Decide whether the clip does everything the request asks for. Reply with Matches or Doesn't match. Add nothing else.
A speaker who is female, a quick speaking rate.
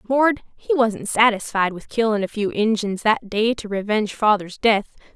Doesn't match